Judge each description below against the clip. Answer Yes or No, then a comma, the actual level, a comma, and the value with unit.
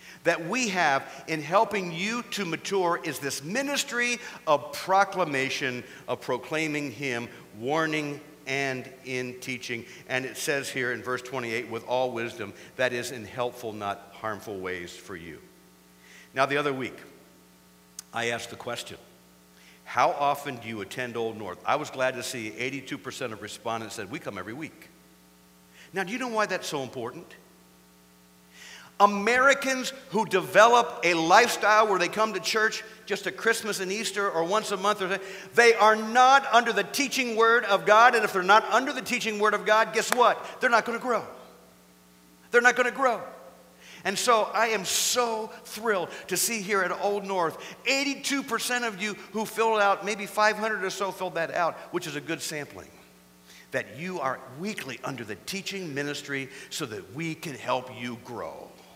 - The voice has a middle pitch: Yes, medium, 165 Hz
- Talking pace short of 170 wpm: No, average, 175 wpm